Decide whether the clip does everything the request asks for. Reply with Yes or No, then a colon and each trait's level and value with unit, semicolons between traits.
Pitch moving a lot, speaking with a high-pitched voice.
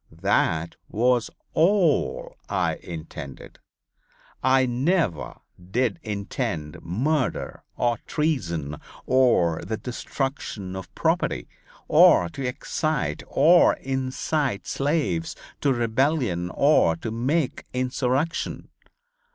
No: wide, 7.4 semitones; low, 125 Hz